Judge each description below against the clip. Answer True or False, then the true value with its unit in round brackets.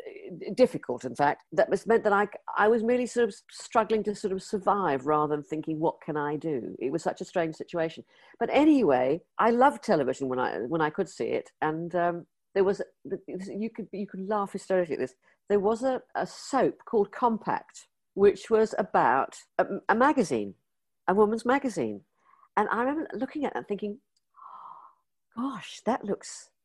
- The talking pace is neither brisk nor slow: True (185 wpm)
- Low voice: False (205 Hz)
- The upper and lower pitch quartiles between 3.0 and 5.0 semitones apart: False (5.6 semitones)